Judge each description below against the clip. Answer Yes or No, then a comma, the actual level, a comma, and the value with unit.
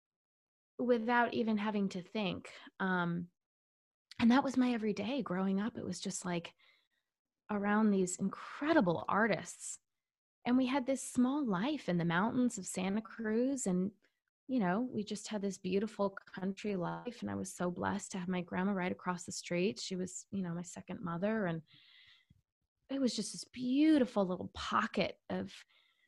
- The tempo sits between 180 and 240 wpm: No, average, 165 wpm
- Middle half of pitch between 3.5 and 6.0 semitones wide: Yes, average, 5.1 semitones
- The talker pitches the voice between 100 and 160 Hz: No, high, 205 Hz